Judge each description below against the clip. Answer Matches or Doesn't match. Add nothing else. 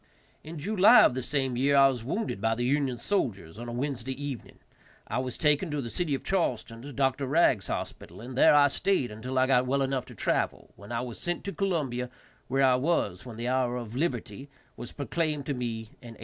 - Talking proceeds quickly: Matches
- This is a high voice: Doesn't match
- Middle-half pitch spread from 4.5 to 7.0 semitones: Doesn't match